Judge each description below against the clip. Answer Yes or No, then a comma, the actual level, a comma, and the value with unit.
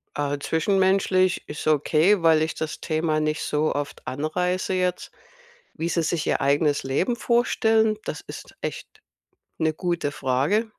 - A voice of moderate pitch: Yes, medium, 160 Hz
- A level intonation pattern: No, average, 3.8 semitones